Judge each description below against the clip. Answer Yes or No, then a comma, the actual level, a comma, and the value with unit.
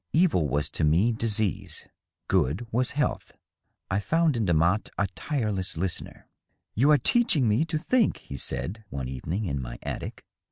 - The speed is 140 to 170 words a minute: Yes, average, 165 wpm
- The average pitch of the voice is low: Yes, low, 105 Hz